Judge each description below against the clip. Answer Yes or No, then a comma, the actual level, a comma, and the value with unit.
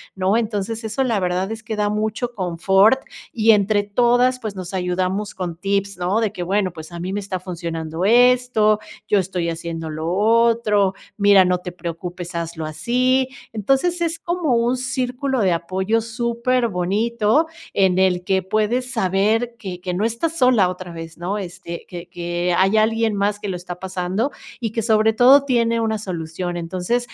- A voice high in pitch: Yes, high, 205 Hz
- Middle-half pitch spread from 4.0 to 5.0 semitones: Yes, average, 4.4 semitones